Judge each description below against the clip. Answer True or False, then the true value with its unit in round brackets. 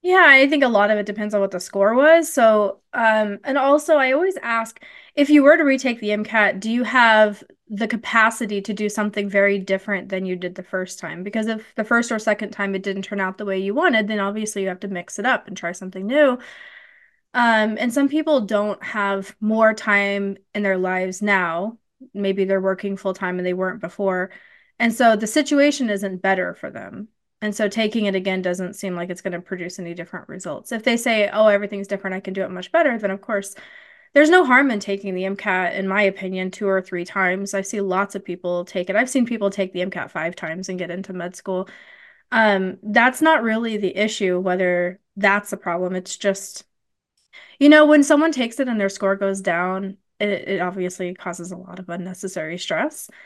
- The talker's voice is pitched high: True (200 Hz)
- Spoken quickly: True (220 wpm)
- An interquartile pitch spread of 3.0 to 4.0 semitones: True (3.5 semitones)